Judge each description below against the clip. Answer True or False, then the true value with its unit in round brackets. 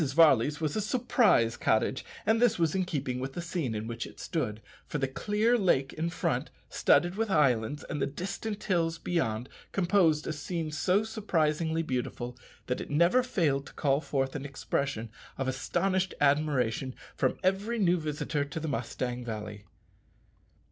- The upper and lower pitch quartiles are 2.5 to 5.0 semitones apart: False (5.5 semitones)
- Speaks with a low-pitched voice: False (150 Hz)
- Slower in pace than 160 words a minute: False (165 wpm)